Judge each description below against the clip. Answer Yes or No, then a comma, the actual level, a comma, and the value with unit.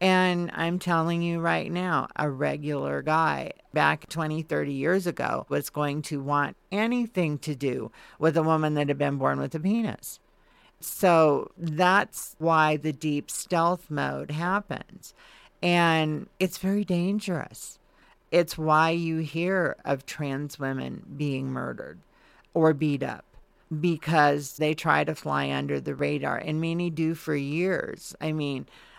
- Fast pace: No, average, 145 wpm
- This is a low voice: No, medium, 160 Hz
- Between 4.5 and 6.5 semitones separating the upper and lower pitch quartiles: No, average, 3.1 semitones